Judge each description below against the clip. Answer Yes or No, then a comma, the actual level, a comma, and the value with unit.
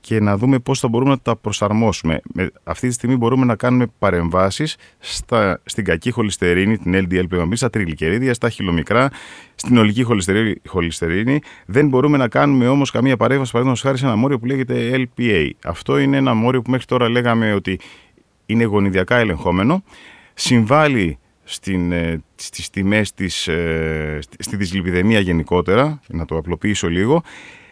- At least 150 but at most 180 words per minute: Yes, average, 155 wpm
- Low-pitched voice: Yes, low, 110 Hz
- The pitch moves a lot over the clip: Yes, wide, 5.9 semitones